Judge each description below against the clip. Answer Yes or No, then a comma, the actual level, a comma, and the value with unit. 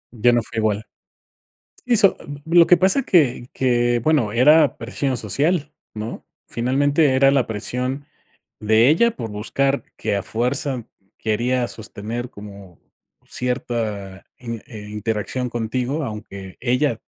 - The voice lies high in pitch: No, low, 120 Hz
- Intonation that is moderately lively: Yes, average, 4.2 semitones